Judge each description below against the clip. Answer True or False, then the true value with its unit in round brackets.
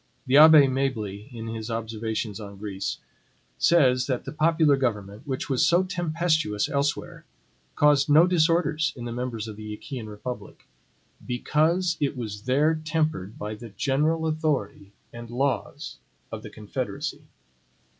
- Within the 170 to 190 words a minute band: False (140 wpm)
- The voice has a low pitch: True (130 Hz)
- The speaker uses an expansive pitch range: True (5.8 semitones)